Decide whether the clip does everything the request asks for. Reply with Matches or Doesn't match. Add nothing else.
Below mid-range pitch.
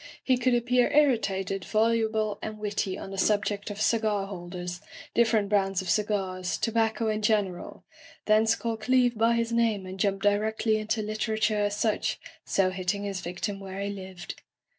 Doesn't match